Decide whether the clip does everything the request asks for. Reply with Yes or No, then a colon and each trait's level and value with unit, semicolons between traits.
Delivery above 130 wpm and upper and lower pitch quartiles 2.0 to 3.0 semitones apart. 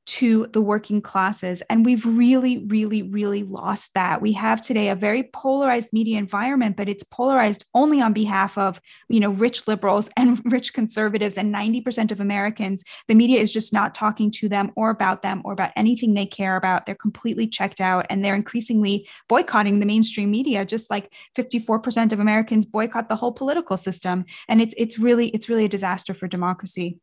Yes: average, 190 wpm; narrow, 2.5 semitones